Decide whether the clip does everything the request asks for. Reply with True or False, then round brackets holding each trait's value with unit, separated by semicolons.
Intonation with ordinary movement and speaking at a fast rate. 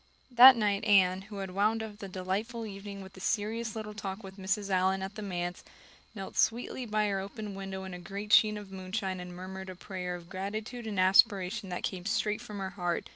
False (2.1 semitones; 215 wpm)